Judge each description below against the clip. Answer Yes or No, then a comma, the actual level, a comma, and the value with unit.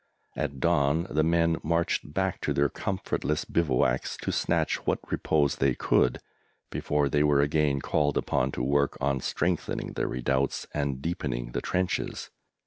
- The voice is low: Yes, very low, 75 Hz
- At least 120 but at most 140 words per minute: No, average, 150 wpm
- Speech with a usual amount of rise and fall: Yes, average, 3.0 semitones